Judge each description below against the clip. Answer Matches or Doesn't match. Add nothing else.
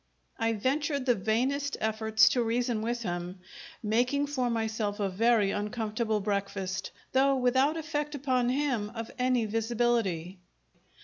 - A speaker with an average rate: Doesn't match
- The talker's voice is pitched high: Matches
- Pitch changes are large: Doesn't match